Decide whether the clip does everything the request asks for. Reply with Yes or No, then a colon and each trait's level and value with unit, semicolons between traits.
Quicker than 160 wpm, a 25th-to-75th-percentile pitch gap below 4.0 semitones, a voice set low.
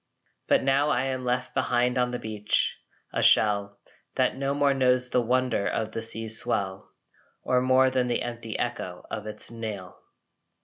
Yes: average, 170 wpm; average, 2.7 semitones; low, 125 Hz